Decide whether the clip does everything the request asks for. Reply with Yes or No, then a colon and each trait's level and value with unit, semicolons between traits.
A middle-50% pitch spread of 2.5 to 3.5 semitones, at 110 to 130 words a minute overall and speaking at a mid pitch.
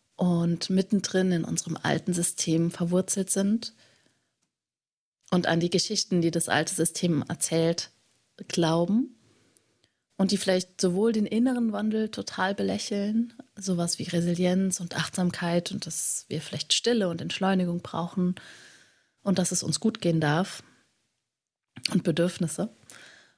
Yes: average, 2.8 semitones; slow, 125 wpm; medium, 180 Hz